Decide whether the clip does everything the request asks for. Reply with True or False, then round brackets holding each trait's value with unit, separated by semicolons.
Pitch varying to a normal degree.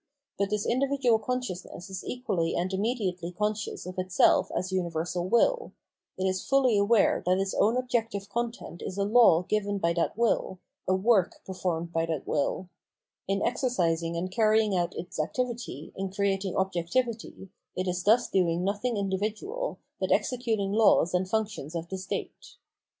True (4.0 semitones)